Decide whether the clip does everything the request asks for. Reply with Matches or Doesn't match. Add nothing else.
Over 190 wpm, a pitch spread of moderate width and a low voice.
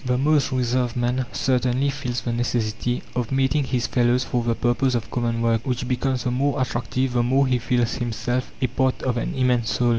Doesn't match